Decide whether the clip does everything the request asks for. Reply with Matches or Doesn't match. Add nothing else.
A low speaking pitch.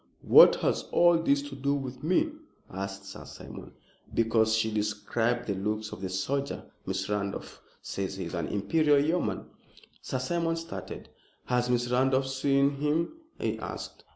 Matches